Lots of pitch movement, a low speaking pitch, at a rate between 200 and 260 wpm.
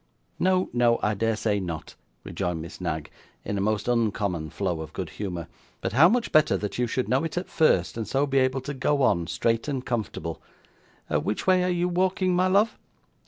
Yes: wide, 8.3 semitones; low, 115 Hz; fast, 205 wpm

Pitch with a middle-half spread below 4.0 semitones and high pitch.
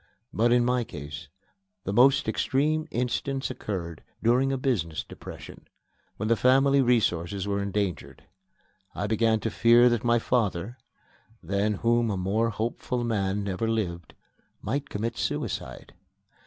No: average, 3.6 semitones; low, 115 Hz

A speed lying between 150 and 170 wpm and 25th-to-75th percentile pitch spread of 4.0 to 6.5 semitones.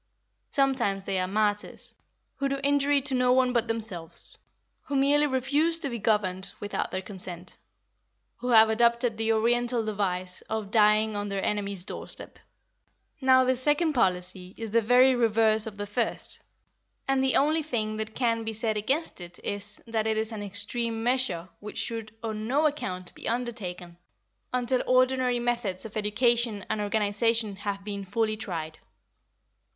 No: average, 160 wpm; average, 3.5 semitones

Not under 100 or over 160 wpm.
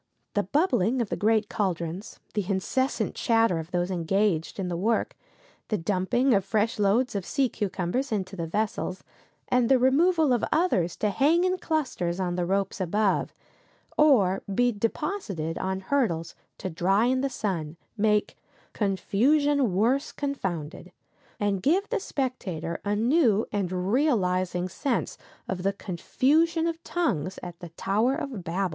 Yes: average, 150 wpm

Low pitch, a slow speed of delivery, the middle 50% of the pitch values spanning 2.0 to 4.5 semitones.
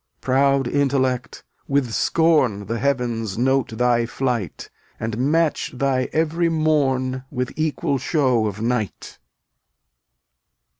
Yes: low, 130 Hz; slow, 105 wpm; average, 2.9 semitones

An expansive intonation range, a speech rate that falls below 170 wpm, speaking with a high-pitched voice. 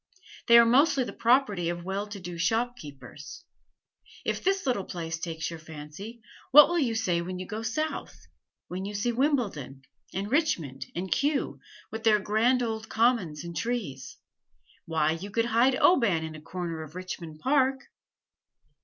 Yes: wide, 6.5 semitones; average, 160 wpm; high, 205 Hz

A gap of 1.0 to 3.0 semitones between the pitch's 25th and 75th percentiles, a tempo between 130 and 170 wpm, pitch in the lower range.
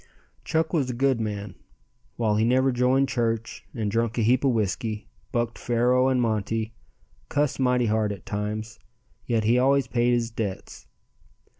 Yes: narrow, 2.6 semitones; average, 160 wpm; low, 115 Hz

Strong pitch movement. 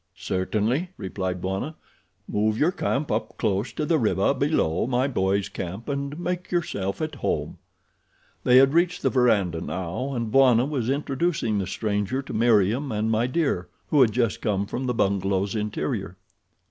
Yes: wide, 5.7 semitones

